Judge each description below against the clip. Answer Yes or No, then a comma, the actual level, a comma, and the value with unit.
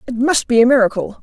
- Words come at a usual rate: No, fast, 245 wpm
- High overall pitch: Yes, high, 240 Hz